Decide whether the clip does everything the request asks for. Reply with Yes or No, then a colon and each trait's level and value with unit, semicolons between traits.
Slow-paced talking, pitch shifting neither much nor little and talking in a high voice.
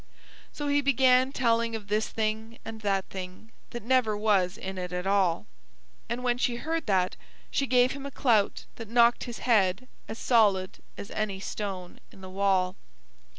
No: average, 175 wpm; average, 4.1 semitones; high, 220 Hz